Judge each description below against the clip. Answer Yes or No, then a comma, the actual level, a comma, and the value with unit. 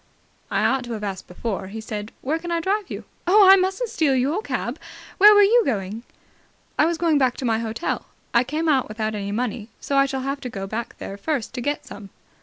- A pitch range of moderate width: No, wide, 7.2 semitones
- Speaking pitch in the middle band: No, very high, 260 Hz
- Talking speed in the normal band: No, fast, 225 wpm